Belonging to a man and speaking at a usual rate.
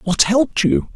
Yes: male; average, 190 wpm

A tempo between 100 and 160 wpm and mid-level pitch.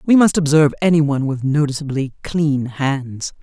Yes: average, 140 wpm; medium, 145 Hz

